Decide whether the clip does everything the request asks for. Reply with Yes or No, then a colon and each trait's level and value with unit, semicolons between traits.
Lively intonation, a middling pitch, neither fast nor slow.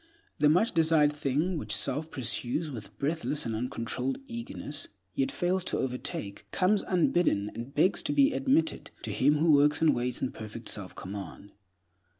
Yes: wide, 6.3 semitones; medium, 145 Hz; average, 160 wpm